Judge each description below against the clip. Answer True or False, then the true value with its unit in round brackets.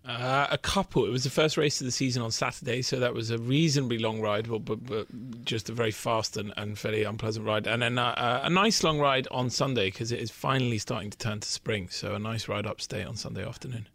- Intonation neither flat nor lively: True (3.5 semitones)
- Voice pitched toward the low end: True (115 Hz)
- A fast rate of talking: True (255 wpm)